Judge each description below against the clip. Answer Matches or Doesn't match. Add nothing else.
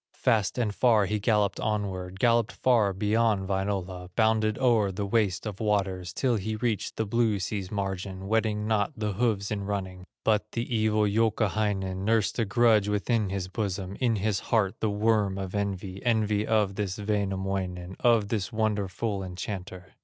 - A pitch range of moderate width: Doesn't match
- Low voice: Matches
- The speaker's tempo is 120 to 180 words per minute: Matches